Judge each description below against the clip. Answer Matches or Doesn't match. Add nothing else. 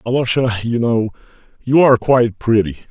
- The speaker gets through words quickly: Doesn't match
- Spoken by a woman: Doesn't match